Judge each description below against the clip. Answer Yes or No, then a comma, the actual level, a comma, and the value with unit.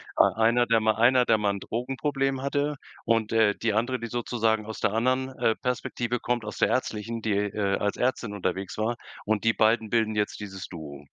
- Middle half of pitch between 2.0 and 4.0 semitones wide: Yes, average, 2.7 semitones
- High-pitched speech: No, low, 110 Hz